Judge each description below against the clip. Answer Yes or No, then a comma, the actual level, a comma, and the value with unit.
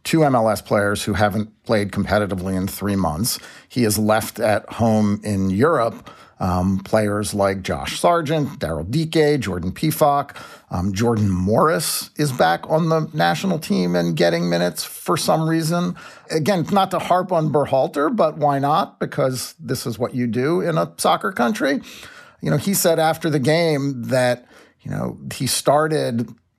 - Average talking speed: Yes, average, 160 wpm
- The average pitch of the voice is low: Yes, low, 120 Hz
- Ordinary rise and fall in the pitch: No, wide, 7.6 semitones